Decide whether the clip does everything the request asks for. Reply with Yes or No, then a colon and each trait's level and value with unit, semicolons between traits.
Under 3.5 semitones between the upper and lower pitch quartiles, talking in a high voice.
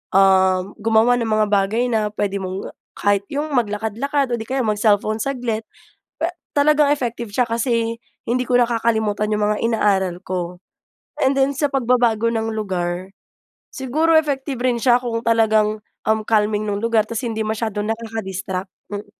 Yes: average, 2.9 semitones; high, 225 Hz